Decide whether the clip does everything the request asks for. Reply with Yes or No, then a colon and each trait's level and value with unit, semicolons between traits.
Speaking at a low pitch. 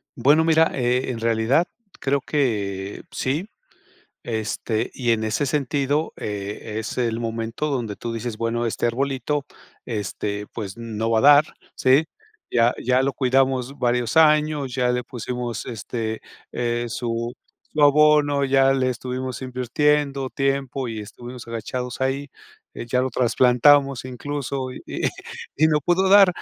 Yes: low, 125 Hz